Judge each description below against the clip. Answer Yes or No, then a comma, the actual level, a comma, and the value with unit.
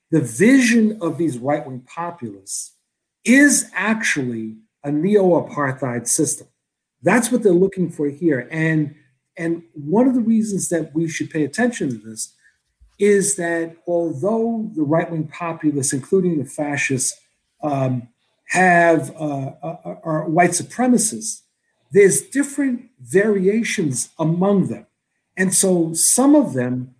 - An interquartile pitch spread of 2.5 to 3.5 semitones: No, wide, 5.6 semitones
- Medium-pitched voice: Yes, medium, 165 Hz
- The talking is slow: Yes, slow, 120 wpm